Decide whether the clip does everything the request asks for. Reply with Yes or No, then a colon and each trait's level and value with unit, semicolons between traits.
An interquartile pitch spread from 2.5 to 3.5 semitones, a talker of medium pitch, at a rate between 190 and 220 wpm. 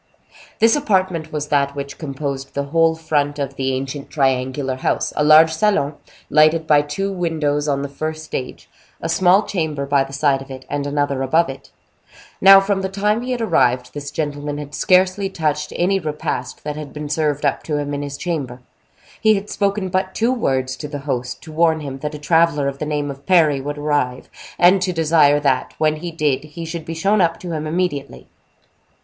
Yes: average, 3.2 semitones; medium, 150 Hz; fast, 205 wpm